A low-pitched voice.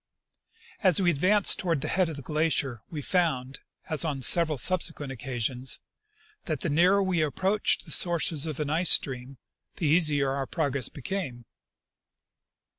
No: medium, 155 Hz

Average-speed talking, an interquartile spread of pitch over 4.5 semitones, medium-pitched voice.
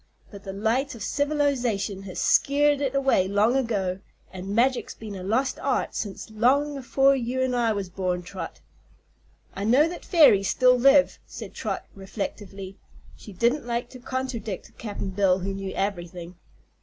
No: average, 160 wpm; average, 5.3 semitones; high, 225 Hz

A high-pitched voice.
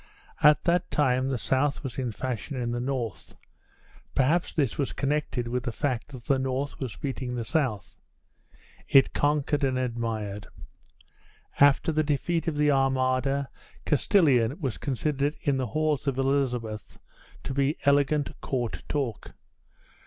No: low, 135 Hz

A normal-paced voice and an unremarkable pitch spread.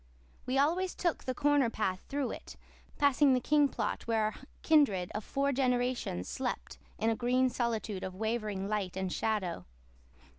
Yes: average, 160 wpm; average, 4.9 semitones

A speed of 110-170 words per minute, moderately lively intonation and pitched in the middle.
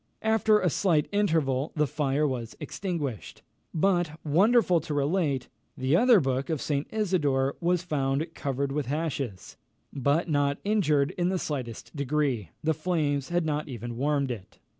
Yes: average, 150 wpm; average, 4.2 semitones; medium, 150 Hz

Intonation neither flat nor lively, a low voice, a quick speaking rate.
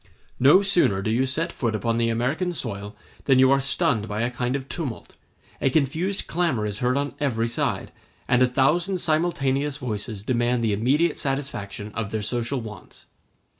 No: average, 4.1 semitones; low, 125 Hz; average, 175 wpm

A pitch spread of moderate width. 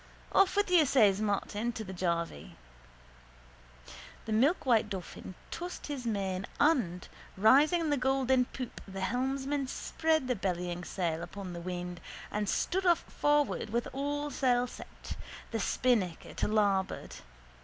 No: wide, 6.5 semitones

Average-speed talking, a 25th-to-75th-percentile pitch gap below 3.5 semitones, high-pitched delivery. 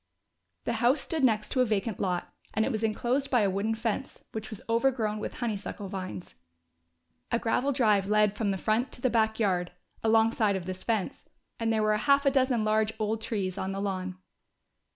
Yes: average, 195 wpm; average, 2.8 semitones; high, 220 Hz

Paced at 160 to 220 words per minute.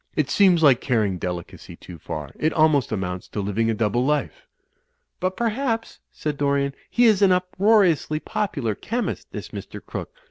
Yes: average, 165 wpm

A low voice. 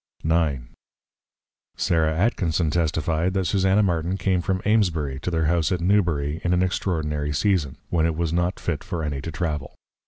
Yes: very low, 85 Hz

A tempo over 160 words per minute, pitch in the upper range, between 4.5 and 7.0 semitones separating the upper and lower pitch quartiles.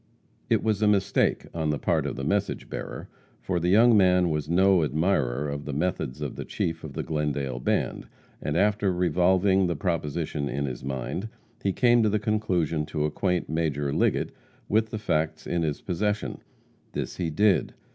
No: average, 180 wpm; very low, 85 Hz; average, 4.8 semitones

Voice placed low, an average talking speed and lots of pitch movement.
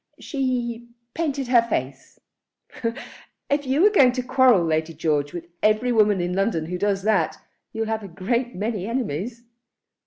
No: high, 220 Hz; average, 150 wpm; wide, 5.7 semitones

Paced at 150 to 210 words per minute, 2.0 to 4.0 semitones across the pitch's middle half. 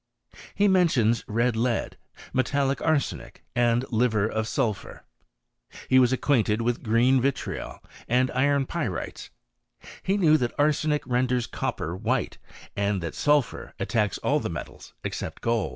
No: slow, 135 wpm; average, 3.7 semitones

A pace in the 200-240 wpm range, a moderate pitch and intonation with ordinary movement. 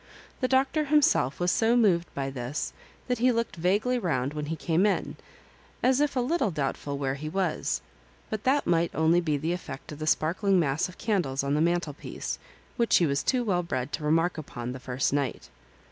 No: fast, 205 wpm; medium, 170 Hz; wide, 7.4 semitones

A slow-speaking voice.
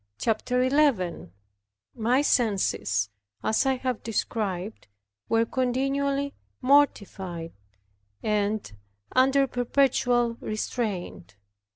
Yes: slow, 75 wpm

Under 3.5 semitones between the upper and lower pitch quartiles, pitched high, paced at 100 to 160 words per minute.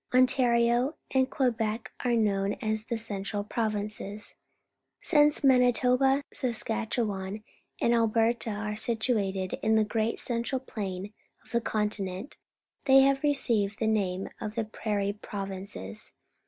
Yes: average, 3.0 semitones; high, 220 Hz; average, 140 wpm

